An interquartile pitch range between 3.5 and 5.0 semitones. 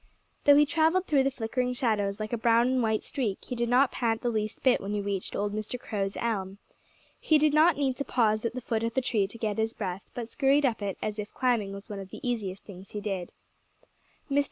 Yes: average, 3.8 semitones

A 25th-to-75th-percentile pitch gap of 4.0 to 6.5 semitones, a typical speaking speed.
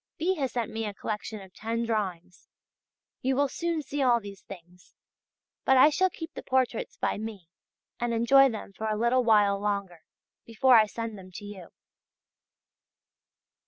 Yes: average, 4.5 semitones; average, 165 wpm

